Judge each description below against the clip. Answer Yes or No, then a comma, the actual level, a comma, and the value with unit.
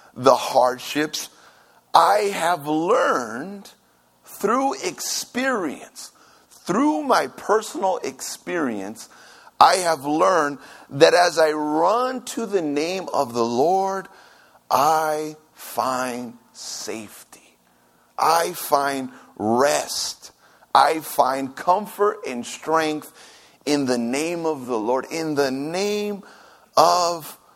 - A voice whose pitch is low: No, medium, 155 Hz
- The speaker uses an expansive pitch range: Yes, wide, 6.1 semitones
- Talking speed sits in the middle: No, slow, 100 wpm